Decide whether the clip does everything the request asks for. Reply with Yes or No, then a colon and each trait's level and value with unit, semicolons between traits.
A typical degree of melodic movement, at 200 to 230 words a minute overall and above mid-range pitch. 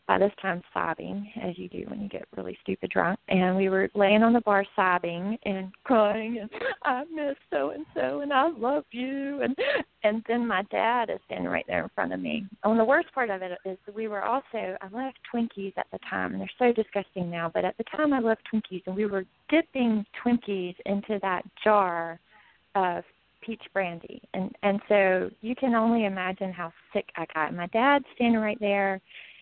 Yes: average, 3.7 semitones; fast, 205 wpm; high, 210 Hz